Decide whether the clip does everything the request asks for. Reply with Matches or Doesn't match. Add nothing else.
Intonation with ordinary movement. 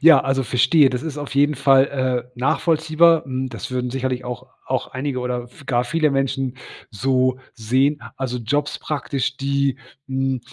Doesn't match